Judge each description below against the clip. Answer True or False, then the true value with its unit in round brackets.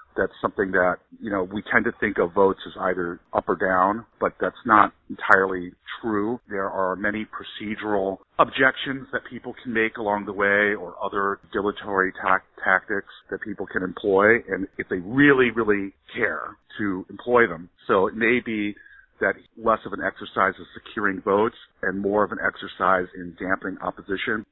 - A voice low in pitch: True (105 Hz)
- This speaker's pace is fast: False (175 wpm)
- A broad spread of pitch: False (2.9 semitones)